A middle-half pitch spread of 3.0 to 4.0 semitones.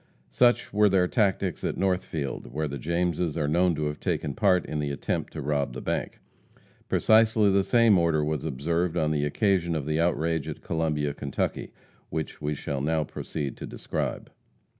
Yes: average, 3.6 semitones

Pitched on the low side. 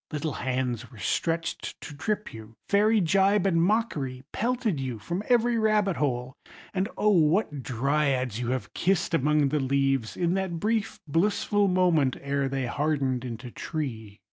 No: medium, 150 Hz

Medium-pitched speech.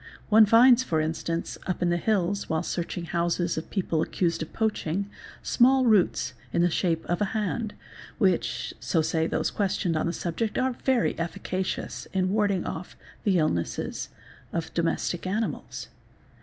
Yes: medium, 180 Hz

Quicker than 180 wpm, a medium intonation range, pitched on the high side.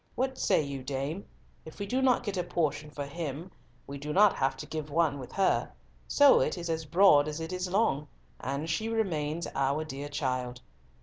No: average, 200 wpm; average, 4.9 semitones; medium, 155 Hz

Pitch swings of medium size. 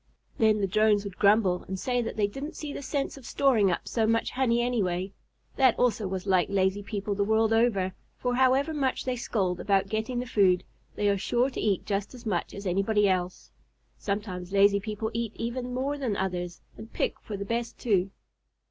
Yes: average, 3.7 semitones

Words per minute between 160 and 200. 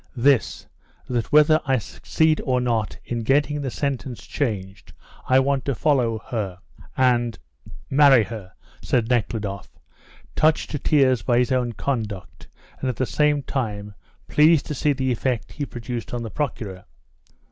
No: average, 150 wpm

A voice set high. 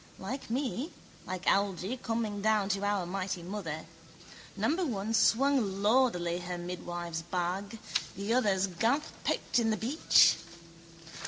Yes: high, 200 Hz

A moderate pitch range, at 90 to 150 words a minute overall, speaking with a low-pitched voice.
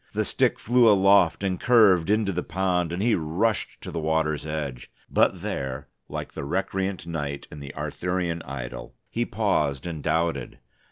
No: average, 4.2 semitones; average, 165 wpm; very low, 85 Hz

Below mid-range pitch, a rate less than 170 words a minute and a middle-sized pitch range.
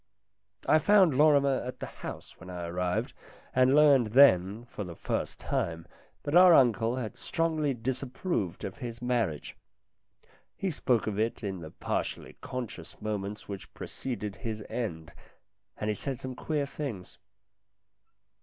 No: low, 120 Hz; average, 145 wpm; wide, 5.8 semitones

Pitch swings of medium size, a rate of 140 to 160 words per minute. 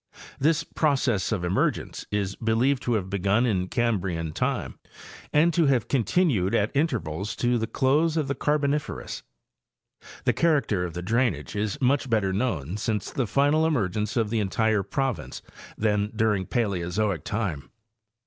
No: wide, 5.8 semitones; average, 150 wpm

